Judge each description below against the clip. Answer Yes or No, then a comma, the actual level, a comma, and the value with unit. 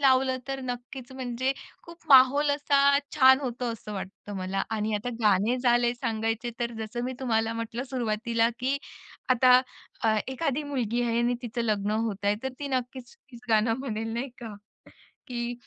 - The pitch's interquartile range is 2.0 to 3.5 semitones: Yes, average, 2.8 semitones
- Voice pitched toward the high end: Yes, high, 240 Hz